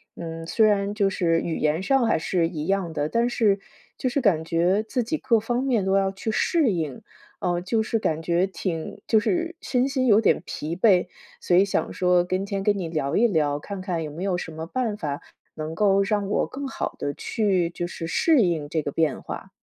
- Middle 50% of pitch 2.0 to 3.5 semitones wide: No, average, 4.8 semitones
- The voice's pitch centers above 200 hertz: No, high, 190 Hz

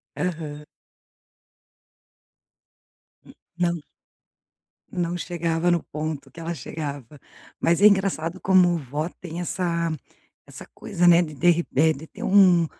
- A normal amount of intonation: No, narrow, 2.1 semitones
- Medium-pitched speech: Yes, medium, 170 Hz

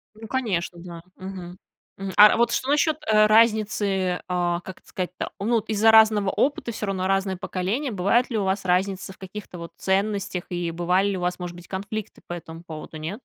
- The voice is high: Yes, high, 195 Hz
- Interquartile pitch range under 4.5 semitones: Yes, average, 3.2 semitones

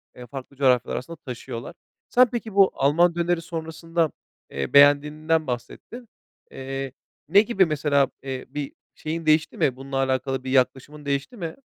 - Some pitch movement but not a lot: Yes, average, 3.9 semitones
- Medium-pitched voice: Yes, medium, 145 Hz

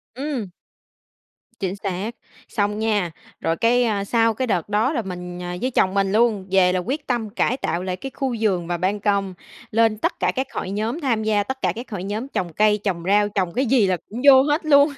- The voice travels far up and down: No, average, 4.4 semitones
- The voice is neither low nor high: No, high, 210 Hz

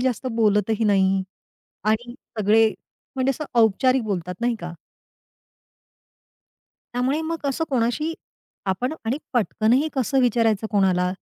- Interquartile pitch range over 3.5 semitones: Yes, average, 4.1 semitones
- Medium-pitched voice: No, high, 230 Hz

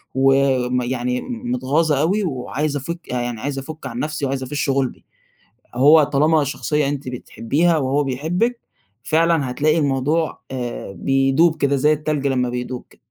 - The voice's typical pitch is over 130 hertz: Yes, medium, 140 Hz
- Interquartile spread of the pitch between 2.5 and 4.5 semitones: Yes, average, 3.1 semitones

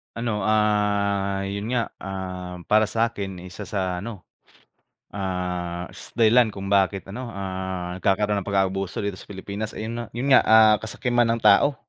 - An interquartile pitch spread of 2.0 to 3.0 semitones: Yes, narrow, 2.5 semitones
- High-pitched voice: No, low, 100 Hz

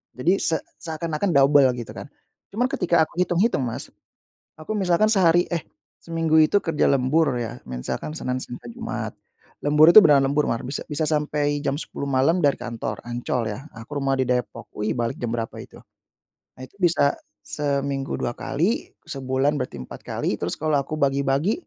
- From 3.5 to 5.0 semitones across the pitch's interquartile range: Yes, average, 4.2 semitones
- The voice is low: No, medium, 145 Hz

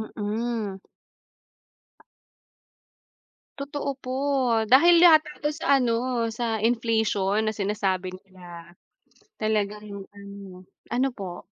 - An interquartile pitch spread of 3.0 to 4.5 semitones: Yes, average, 3.6 semitones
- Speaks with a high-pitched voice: Yes, high, 215 Hz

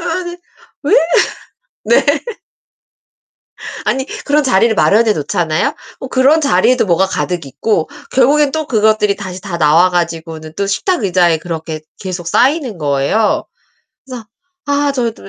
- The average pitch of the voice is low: No, high, 205 Hz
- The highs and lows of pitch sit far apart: Yes, wide, 7.6 semitones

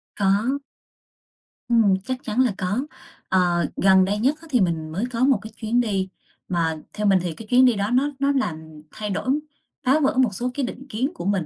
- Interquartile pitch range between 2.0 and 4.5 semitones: No, average, 5.3 semitones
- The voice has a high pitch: Yes, high, 215 Hz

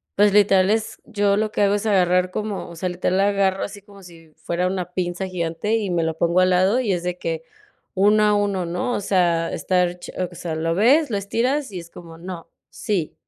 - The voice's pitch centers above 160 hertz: Yes, medium, 185 Hz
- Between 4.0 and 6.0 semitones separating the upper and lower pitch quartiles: No, average, 2.7 semitones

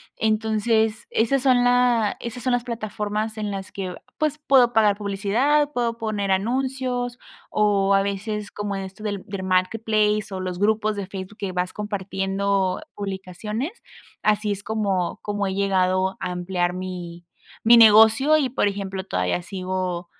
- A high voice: Yes, high, 205 Hz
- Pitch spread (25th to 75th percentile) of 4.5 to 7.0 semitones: No, average, 2.8 semitones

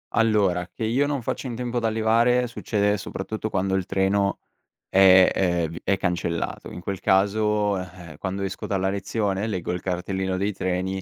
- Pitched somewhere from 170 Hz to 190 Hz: No, very low, 95 Hz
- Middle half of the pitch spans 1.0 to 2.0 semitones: No, average, 2.7 semitones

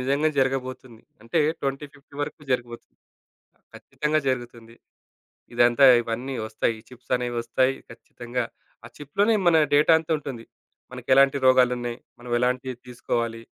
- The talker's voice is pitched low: Yes, low, 125 Hz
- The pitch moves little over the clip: Yes, narrow, 2.3 semitones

